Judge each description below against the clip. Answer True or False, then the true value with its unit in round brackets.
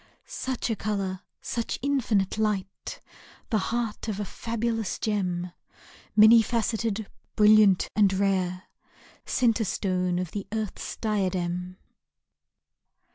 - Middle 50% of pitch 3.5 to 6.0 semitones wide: False (3.1 semitones)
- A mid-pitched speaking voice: False (210 Hz)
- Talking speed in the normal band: False (105 wpm)